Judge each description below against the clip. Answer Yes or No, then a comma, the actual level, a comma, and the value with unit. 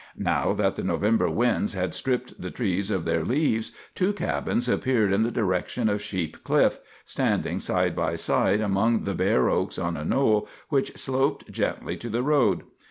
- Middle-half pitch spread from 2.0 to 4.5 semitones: No, average, 5.1 semitones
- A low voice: Yes, low, 105 Hz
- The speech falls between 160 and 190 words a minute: Yes, average, 175 wpm